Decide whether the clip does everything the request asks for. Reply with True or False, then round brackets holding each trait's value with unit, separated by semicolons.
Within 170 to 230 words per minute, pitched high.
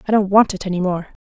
False (295 wpm; 195 Hz)